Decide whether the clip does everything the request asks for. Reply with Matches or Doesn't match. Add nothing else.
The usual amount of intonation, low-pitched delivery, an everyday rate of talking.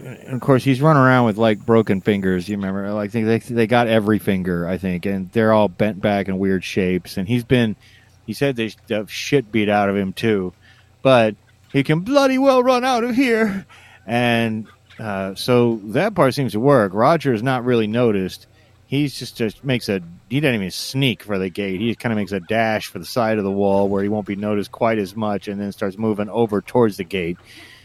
Doesn't match